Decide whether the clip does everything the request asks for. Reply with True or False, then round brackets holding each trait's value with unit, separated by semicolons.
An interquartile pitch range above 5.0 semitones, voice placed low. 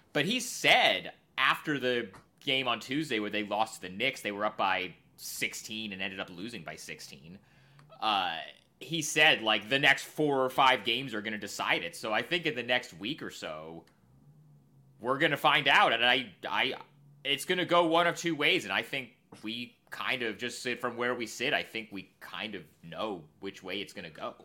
True (5.5 semitones; 125 Hz)